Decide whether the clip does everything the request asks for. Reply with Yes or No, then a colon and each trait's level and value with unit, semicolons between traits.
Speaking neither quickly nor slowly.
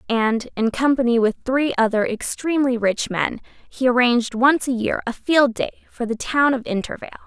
Yes: average, 180 wpm